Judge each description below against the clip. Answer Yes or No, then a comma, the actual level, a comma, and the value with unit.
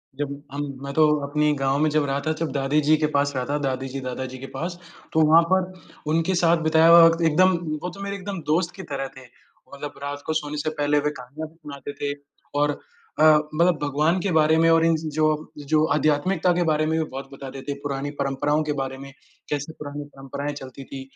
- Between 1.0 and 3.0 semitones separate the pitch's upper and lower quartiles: Yes, narrow, 2.6 semitones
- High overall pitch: No, medium, 150 Hz